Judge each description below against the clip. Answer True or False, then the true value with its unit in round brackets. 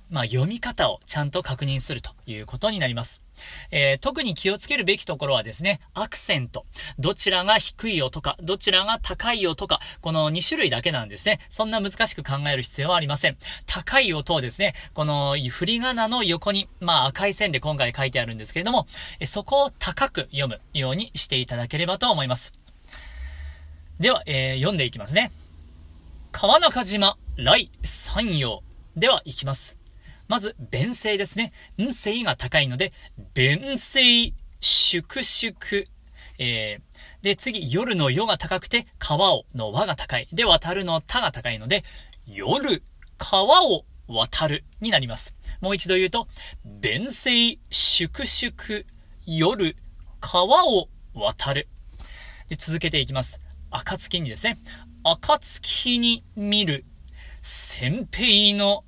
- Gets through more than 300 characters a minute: False (270 characters per minute)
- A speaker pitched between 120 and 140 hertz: False (165 Hz)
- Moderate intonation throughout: False (8.2 semitones)